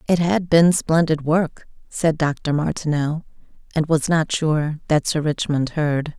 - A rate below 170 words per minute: Yes, average, 155 wpm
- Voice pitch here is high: No, medium, 155 Hz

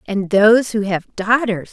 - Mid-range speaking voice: No, high, 210 Hz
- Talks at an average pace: Yes, average, 175 wpm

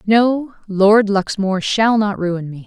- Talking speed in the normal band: Yes, average, 155 wpm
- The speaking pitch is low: No, high, 205 Hz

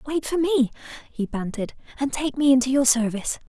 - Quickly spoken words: No, average, 185 wpm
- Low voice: No, very high, 265 Hz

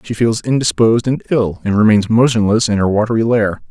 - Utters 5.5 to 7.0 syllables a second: Yes, 5.8 syllables/s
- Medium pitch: No, low, 110 Hz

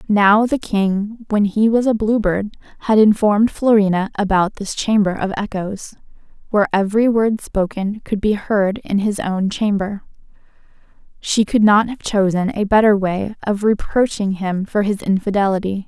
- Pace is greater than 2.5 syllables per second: Yes, 4.6 syllables/s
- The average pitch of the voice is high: Yes, high, 205 Hz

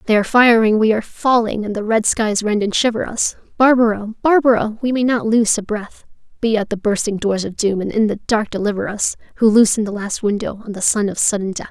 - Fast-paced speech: Yes, fast, 235 wpm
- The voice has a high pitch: Yes, high, 215 Hz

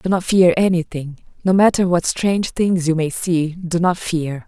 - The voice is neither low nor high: Yes, medium, 175 Hz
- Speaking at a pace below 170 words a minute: No, average, 200 wpm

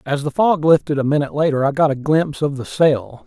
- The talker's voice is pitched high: No, medium, 145 Hz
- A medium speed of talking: No, fast, 255 wpm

